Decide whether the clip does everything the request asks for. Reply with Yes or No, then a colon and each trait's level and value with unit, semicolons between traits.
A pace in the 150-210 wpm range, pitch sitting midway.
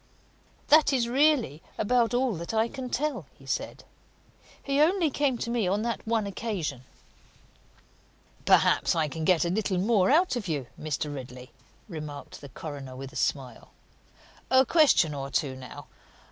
No: average, 160 wpm; high, 200 Hz